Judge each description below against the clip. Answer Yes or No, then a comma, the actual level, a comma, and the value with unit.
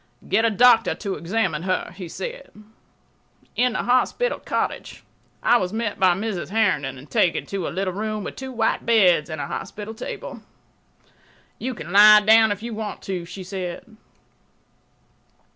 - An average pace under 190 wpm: Yes, average, 160 wpm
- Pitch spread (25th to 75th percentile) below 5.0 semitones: Yes, average, 3.5 semitones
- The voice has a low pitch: No, high, 205 Hz